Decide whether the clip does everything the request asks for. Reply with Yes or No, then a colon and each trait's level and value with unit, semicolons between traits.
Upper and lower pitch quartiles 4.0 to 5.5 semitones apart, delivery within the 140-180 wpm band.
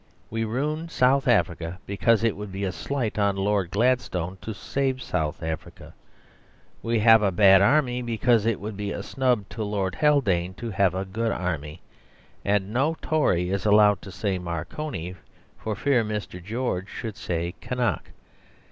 Yes: average, 4.4 semitones; average, 165 wpm